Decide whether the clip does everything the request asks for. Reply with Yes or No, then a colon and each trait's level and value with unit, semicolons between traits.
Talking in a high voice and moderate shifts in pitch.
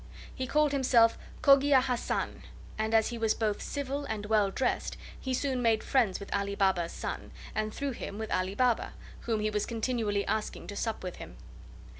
Yes: high, 225 Hz; average, 3.8 semitones